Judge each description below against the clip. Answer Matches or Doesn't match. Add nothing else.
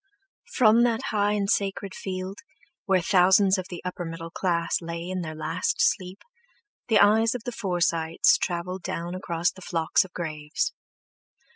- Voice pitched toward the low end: Doesn't match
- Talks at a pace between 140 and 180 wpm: Matches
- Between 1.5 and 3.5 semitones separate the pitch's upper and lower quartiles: Matches